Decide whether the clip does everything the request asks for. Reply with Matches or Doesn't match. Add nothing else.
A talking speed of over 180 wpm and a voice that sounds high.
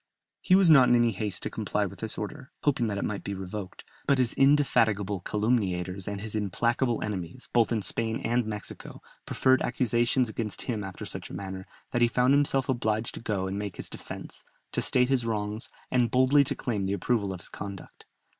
Doesn't match